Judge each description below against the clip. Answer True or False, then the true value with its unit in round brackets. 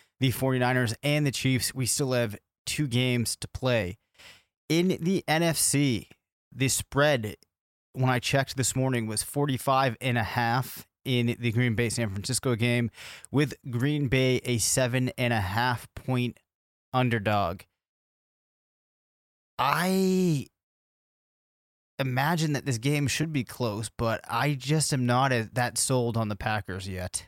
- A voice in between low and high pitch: False (125 Hz)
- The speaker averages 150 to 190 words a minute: False (140 wpm)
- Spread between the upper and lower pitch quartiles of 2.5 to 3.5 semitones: True (3.2 semitones)